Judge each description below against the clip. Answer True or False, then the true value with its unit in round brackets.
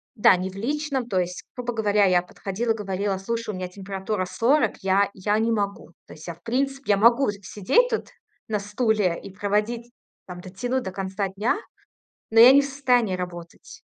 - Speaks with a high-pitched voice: True (205 Hz)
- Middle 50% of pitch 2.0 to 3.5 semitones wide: False (4.0 semitones)